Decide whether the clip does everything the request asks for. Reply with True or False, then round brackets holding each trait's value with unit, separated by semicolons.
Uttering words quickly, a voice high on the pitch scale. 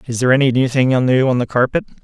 False (235 wpm; 130 Hz)